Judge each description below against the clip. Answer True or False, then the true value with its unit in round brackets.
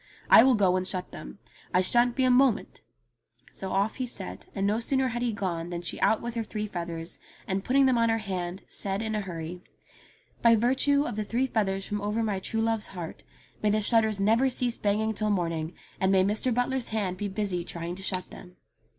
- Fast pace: True (225 wpm)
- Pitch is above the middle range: True (210 Hz)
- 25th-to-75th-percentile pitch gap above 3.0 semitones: True (3.7 semitones)